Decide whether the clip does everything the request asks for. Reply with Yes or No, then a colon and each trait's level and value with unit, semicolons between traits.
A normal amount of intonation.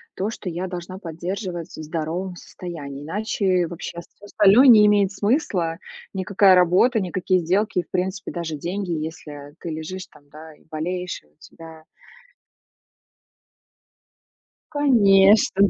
Yes: average, 3.3 semitones